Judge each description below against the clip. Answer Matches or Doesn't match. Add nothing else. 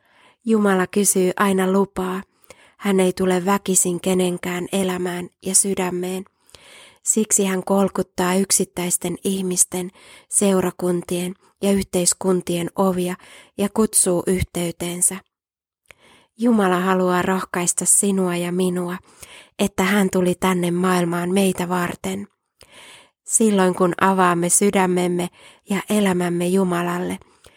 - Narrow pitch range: Matches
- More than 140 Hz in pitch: Matches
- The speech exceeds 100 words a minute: Doesn't match